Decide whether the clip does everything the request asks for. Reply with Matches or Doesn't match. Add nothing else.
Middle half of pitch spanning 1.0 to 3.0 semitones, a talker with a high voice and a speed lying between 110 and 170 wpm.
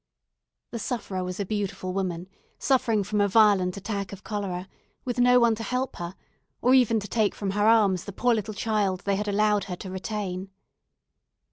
Doesn't match